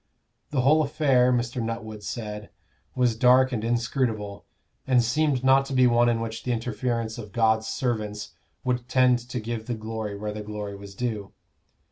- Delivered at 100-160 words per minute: No, average, 170 wpm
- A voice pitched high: No, low, 115 Hz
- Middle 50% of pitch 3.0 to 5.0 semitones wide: No, narrow, 2.6 semitones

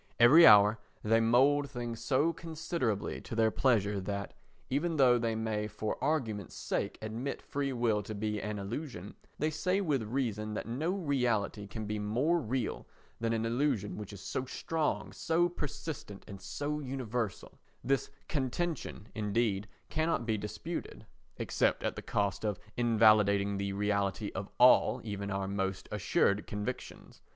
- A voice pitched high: No, low, 115 Hz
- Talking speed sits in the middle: Yes, average, 150 wpm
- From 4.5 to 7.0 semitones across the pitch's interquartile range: Yes, average, 5.0 semitones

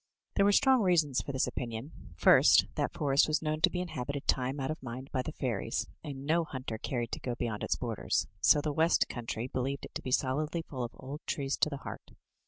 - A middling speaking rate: No, fast, 240 wpm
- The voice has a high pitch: No, low, 135 Hz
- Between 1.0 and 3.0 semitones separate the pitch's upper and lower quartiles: No, average, 3.6 semitones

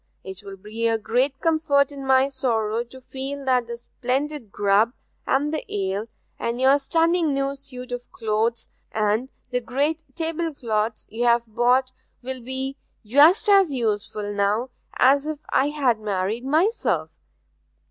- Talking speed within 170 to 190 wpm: No, average, 145 wpm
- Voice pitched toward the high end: Yes, very high, 255 Hz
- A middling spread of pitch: Yes, average, 4.0 semitones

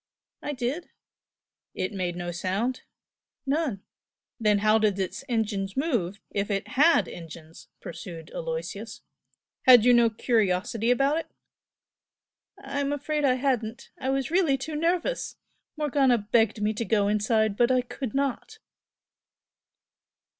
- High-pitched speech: Yes, high, 235 Hz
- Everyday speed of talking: No, slow, 130 wpm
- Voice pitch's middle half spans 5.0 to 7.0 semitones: Yes, average, 5.3 semitones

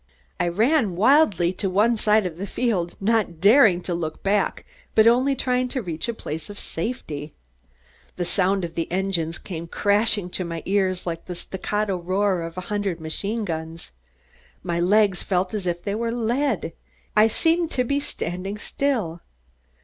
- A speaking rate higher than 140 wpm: Yes, average, 170 wpm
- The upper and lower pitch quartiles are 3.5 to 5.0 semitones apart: Yes, average, 4.3 semitones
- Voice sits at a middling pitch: No, high, 195 Hz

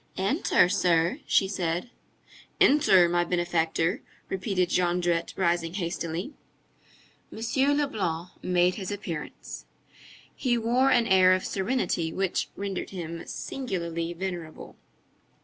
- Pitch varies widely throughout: No, average, 3.1 semitones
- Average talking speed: No, slow, 105 wpm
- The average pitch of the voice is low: No, medium, 180 Hz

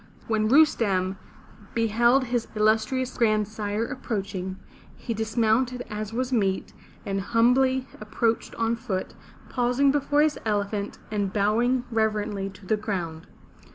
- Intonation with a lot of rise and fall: No, average, 3.1 semitones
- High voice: Yes, high, 220 Hz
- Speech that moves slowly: Yes, slow, 120 wpm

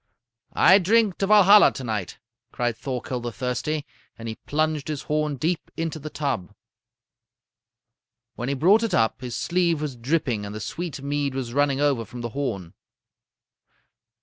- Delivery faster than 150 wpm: Yes, average, 160 wpm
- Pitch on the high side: No, medium, 140 Hz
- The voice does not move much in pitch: No, average, 4.6 semitones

